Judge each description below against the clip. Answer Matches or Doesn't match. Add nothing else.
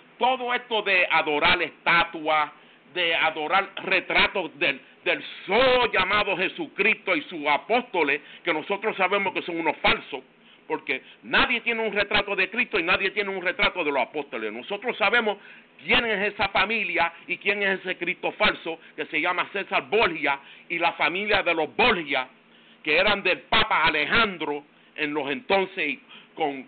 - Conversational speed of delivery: Matches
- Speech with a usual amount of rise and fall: Matches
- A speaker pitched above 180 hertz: Matches